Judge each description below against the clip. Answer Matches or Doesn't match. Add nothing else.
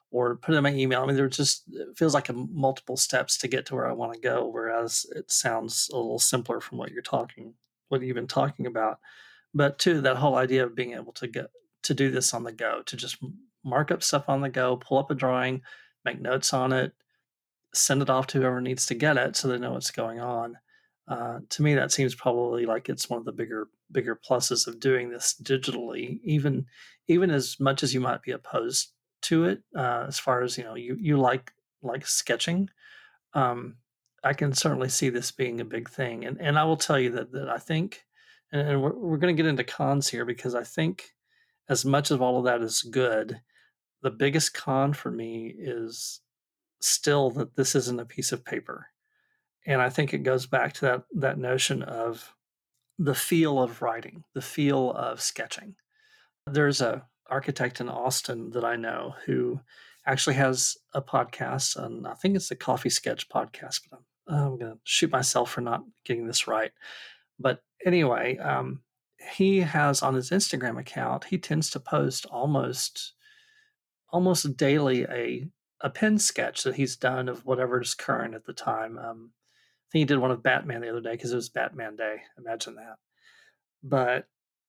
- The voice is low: Matches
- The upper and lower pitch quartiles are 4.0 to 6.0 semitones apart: Doesn't match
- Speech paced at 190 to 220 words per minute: Matches